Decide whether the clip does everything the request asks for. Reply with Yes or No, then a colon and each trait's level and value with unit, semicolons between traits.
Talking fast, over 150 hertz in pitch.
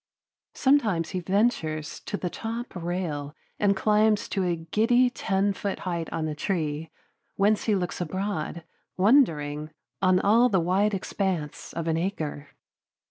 No: slow, 135 wpm; medium, 185 Hz